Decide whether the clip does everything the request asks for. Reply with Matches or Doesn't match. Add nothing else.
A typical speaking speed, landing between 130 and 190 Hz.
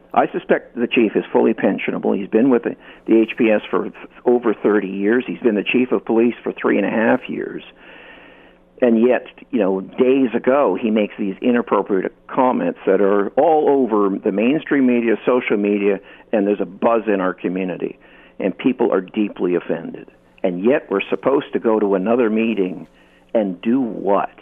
Doesn't match